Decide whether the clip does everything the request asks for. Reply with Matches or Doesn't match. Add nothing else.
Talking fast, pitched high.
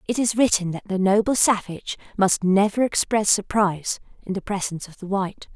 Doesn't match